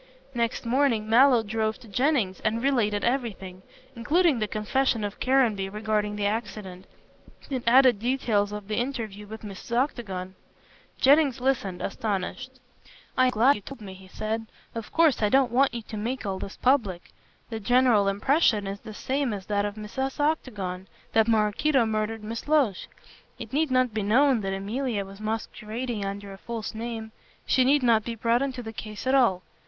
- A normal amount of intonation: Yes, average, 3.8 semitones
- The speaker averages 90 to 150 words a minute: No, average, 175 wpm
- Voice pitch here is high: Yes, high, 225 Hz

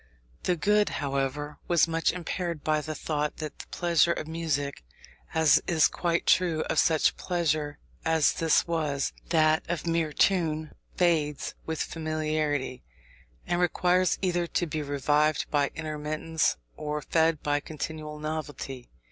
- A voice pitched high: No, medium, 155 Hz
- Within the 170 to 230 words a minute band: No, average, 140 wpm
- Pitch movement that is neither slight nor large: No, narrow, 2.0 semitones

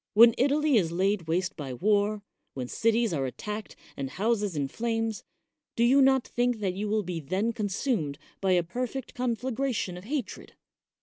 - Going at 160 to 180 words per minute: Yes, average, 170 wpm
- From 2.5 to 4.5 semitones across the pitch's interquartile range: No, average, 4.9 semitones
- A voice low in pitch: No, high, 210 Hz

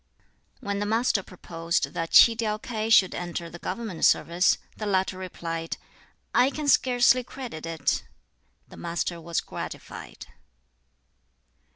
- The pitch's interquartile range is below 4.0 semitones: No, average, 5.1 semitones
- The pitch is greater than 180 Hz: Yes, high, 190 Hz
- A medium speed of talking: No, slow, 130 wpm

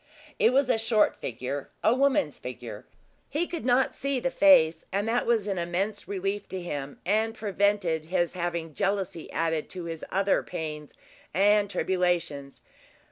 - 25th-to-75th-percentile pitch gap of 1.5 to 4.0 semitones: No, average, 5.0 semitones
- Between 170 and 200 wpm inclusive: No, average, 155 wpm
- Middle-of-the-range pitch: No, high, 195 Hz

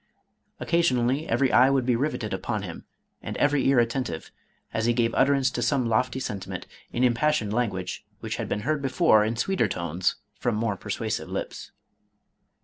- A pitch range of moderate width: Yes, average, 4.0 semitones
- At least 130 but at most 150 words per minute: No, average, 165 wpm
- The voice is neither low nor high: No, low, 120 Hz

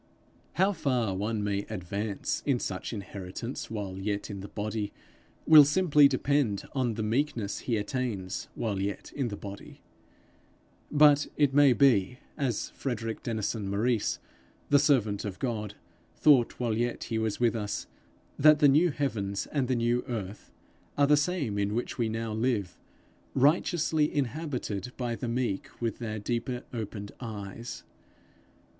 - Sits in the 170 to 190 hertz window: No, low, 115 Hz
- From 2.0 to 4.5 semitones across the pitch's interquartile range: No, average, 5.0 semitones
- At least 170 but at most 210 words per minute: No, average, 150 wpm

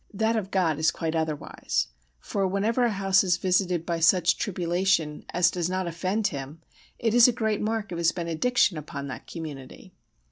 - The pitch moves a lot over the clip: No, average, 3.6 semitones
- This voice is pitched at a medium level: Yes, medium, 180 Hz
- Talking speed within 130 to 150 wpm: No, average, 180 wpm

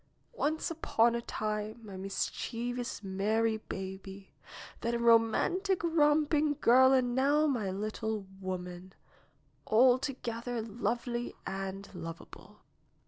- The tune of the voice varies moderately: Yes, average, 4.8 semitones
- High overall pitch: Yes, high, 230 Hz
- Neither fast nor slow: No, slow, 105 wpm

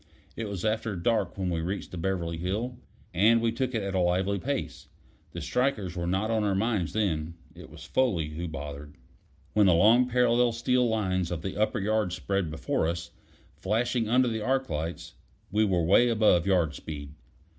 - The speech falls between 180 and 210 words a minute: Yes, average, 190 wpm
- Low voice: Yes, low, 100 Hz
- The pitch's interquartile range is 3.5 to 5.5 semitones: Yes, average, 4.9 semitones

